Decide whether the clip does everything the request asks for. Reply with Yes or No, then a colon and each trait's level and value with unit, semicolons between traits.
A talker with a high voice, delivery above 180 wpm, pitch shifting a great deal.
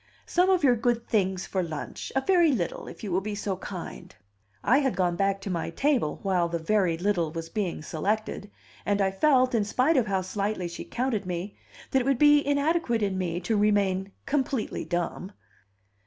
Yes: high, 205 Hz; average, 195 wpm; wide, 5.7 semitones